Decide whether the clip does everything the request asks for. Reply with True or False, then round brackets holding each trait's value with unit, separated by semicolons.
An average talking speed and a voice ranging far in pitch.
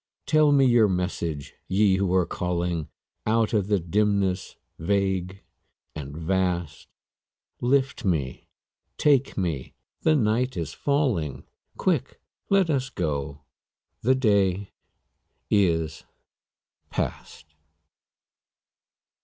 False (95 wpm; 6.1 semitones)